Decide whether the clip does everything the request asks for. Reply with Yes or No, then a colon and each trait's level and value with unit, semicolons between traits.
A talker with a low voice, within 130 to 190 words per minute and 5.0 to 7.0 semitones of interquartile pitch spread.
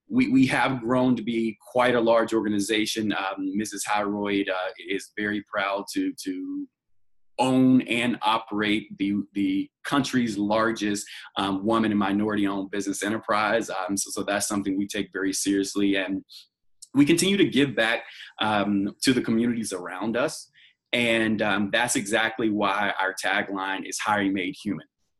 No: low, 105 Hz; average, 150 wpm; average, 2.7 semitones